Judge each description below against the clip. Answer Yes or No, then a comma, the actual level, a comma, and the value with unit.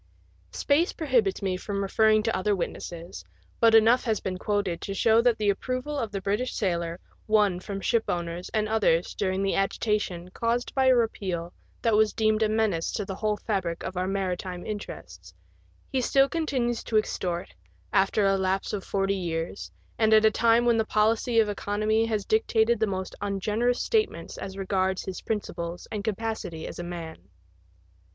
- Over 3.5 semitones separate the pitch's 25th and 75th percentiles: No, average, 3.1 semitones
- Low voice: No, high, 205 Hz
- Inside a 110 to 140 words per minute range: No, average, 175 wpm